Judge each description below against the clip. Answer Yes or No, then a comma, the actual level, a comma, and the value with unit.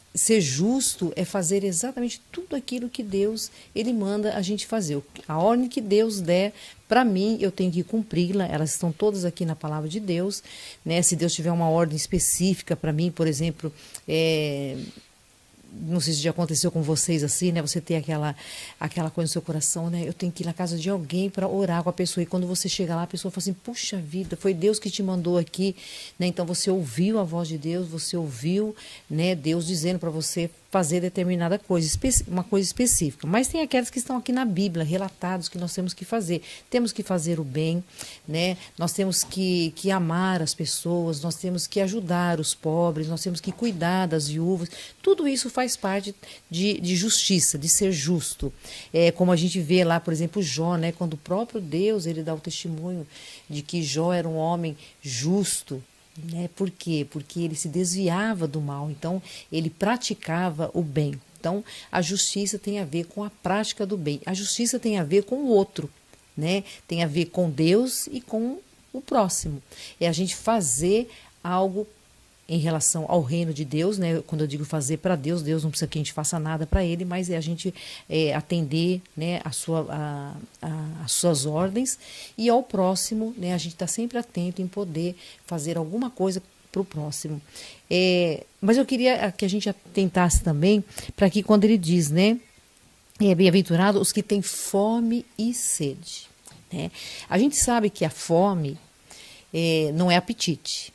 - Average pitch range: Yes, average, 3.4 semitones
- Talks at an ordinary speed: No, fast, 195 wpm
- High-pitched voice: No, medium, 180 Hz